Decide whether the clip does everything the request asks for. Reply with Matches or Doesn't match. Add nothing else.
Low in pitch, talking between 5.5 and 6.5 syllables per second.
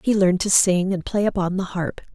Doesn't match